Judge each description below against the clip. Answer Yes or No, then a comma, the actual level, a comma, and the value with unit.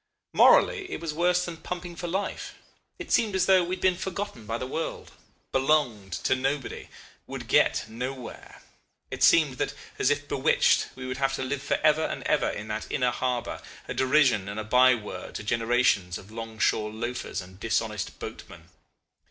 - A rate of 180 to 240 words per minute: Yes, average, 185 wpm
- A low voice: Yes, low, 130 Hz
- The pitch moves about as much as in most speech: No, wide, 6.3 semitones